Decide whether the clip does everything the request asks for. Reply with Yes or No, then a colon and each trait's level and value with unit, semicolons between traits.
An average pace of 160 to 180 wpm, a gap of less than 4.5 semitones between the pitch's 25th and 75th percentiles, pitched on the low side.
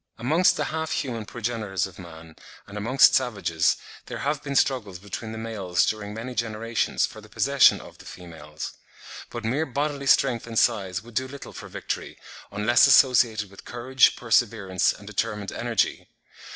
Yes: average, 165 wpm; average, 3.9 semitones; low, 115 Hz